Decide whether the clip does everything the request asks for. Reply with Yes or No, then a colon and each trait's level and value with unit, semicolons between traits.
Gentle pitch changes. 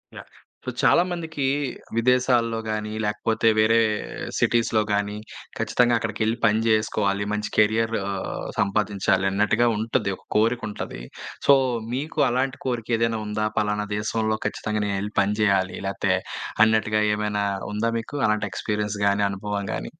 Yes: narrow, 1.8 semitones